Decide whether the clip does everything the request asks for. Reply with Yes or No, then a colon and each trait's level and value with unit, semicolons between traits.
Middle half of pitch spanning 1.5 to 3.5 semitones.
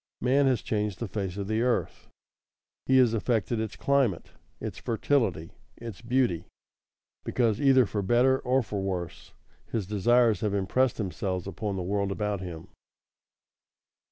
No: average, 4.0 semitones